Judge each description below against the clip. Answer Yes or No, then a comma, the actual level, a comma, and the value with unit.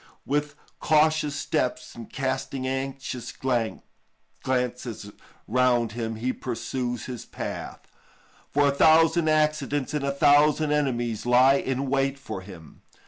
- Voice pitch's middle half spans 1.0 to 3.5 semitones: Yes, average, 3.1 semitones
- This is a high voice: No, low, 135 Hz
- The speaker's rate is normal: No, slow, 120 wpm